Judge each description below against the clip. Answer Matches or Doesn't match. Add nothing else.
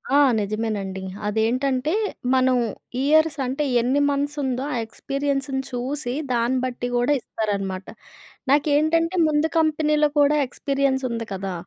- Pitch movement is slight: Doesn't match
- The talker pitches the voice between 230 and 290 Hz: Matches